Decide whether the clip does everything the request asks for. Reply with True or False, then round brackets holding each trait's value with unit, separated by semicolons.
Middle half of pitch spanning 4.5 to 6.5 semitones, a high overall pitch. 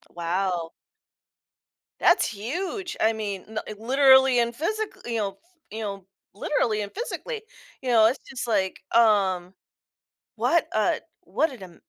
True (5.1 semitones; 220 Hz)